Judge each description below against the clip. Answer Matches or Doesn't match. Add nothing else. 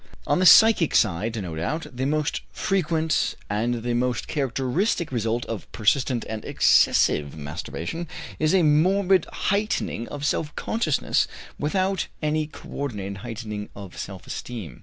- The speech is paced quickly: Doesn't match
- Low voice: Matches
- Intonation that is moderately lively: Doesn't match